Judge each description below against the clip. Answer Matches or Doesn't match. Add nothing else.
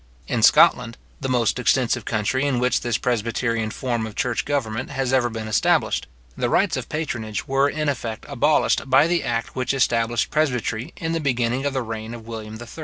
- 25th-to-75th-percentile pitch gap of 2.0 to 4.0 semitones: Matches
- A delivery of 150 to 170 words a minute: Doesn't match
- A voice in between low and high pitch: Doesn't match